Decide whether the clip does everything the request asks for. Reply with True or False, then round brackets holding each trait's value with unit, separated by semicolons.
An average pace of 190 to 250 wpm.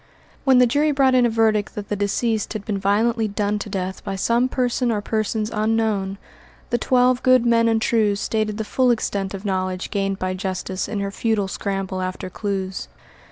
True (195 wpm)